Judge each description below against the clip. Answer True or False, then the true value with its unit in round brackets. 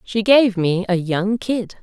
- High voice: True (205 Hz)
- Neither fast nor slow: True (195 wpm)